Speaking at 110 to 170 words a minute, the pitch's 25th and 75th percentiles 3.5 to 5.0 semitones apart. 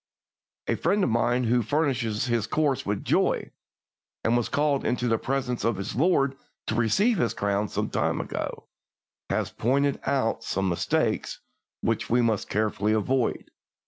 Yes: average, 155 wpm; average, 3.9 semitones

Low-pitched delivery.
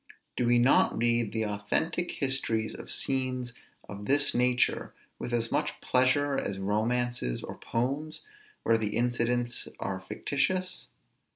Yes: low, 120 Hz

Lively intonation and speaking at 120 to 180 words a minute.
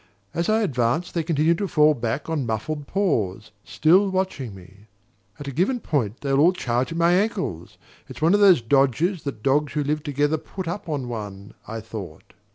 No: wide, 6.5 semitones; average, 190 wpm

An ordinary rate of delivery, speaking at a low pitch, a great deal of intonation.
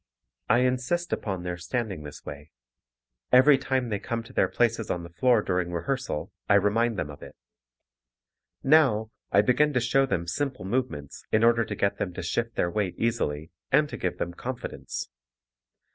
Yes: average, 175 wpm; low, 110 Hz; wide, 6.2 semitones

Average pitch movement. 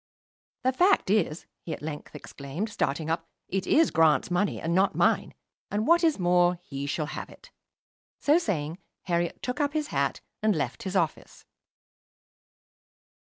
No: wide, 5.7 semitones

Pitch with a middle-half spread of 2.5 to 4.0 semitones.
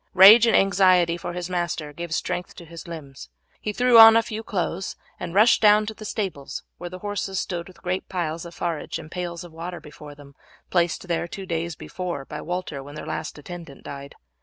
Yes: average, 2.8 semitones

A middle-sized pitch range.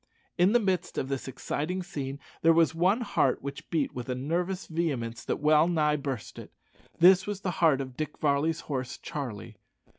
Yes: average, 4.6 semitones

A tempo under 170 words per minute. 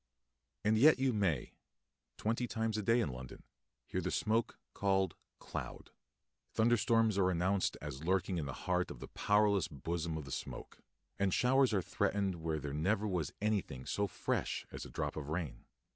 No: average, 175 wpm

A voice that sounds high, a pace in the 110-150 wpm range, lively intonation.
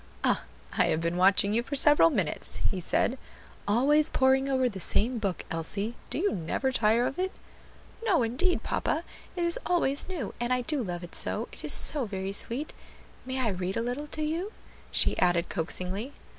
No: high, 240 Hz; average, 190 wpm; wide, 7.2 semitones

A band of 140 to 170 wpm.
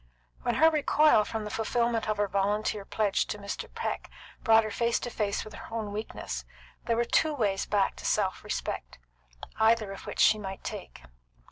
No: average, 190 wpm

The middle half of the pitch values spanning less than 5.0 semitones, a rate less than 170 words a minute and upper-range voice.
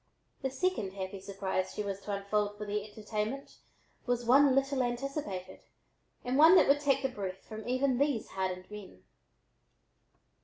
No: average, 5.3 semitones; average, 155 wpm; high, 215 Hz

